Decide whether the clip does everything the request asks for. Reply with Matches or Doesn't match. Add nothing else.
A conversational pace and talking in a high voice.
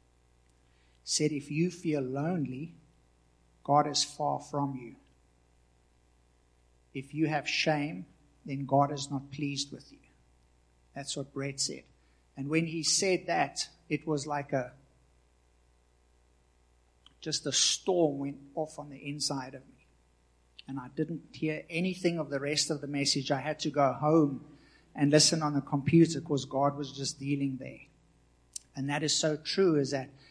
Doesn't match